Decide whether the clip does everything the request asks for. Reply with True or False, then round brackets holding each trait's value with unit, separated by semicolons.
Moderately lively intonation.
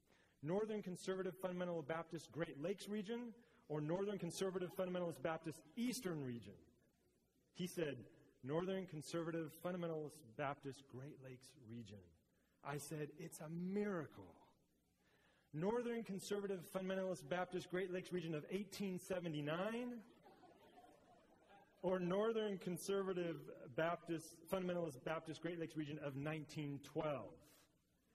True (3.7 semitones)